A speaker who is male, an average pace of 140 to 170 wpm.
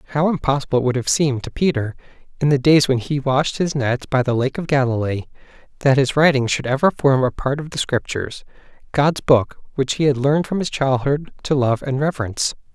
No: male; fast, 205 wpm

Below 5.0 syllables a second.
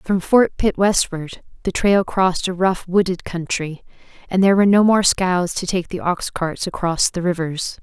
Yes: 4.7 syllables/s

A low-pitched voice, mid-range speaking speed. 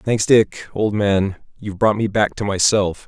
Yes: low, 105 Hz; average, 195 wpm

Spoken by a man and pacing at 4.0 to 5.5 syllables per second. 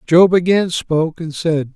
Yes: male; 4.3 syllables/s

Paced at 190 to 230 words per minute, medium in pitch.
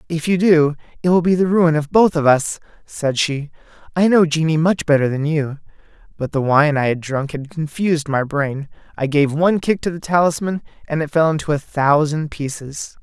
Yes: fast, 205 wpm; medium, 155 Hz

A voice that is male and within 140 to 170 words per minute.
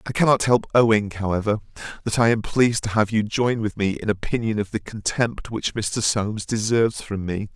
No: male; fast, 205 wpm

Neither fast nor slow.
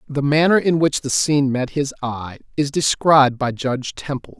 Yes: average, 190 wpm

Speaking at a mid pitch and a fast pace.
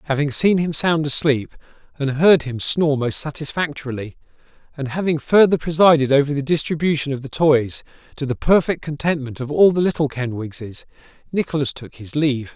No: medium, 145 Hz; average, 160 wpm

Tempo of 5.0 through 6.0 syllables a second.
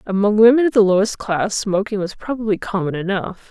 Yes: 5.6 syllables/s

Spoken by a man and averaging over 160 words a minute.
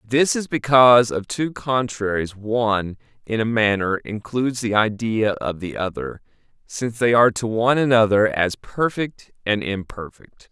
No: male; average, 150 wpm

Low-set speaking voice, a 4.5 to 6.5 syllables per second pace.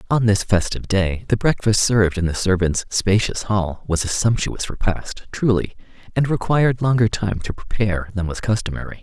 Yes: low, 105 Hz; 5.2 syllables/s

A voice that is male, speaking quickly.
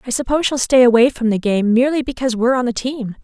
No: female; fast, 295 wpm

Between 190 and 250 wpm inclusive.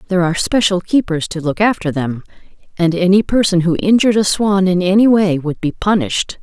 Yes: average, 195 wpm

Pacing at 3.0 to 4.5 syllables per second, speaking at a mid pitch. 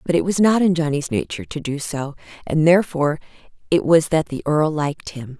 No: 5.9 syllables/s; medium, 155 Hz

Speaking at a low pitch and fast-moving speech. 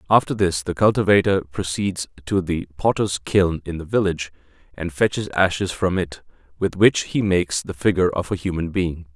No: very low, 90 Hz; average, 175 wpm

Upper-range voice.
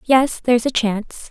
Yes: high, 240 Hz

